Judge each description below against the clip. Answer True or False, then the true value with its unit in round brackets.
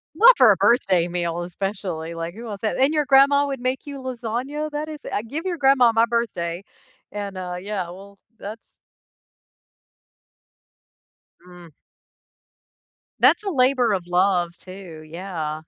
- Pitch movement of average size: False (7.0 semitones)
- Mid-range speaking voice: False (205 Hz)